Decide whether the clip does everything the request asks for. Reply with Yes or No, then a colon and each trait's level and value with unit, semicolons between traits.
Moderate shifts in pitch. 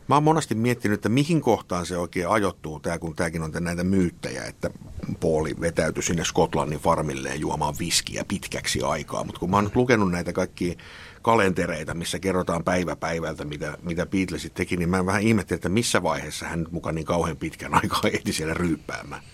Yes: average, 3.5 semitones